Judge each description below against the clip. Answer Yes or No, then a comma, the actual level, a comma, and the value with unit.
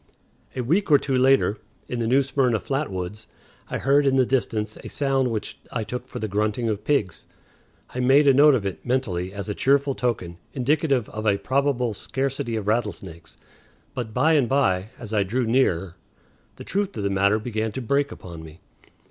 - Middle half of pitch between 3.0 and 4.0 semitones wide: No, average, 4.6 semitones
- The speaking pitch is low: Yes, low, 120 Hz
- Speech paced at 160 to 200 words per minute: Yes, average, 195 wpm